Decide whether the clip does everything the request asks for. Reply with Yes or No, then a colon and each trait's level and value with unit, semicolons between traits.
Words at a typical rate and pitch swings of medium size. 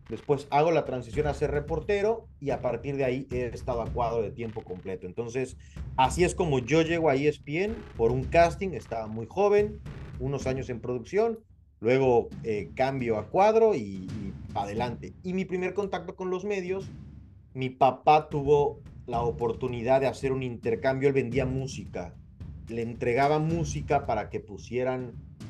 No: average, 165 wpm; wide, 5.8 semitones